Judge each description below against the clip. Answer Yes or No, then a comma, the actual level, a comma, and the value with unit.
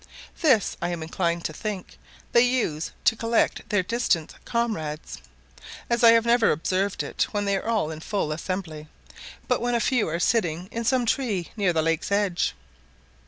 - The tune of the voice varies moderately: No, wide, 5.8 semitones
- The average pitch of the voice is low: No, high, 200 Hz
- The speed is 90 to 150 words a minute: No, average, 175 wpm